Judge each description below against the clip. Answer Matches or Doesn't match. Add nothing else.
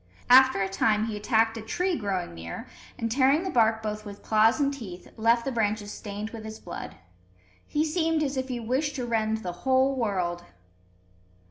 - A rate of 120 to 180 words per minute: Doesn't match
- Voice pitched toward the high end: Matches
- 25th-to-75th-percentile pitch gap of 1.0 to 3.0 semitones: Doesn't match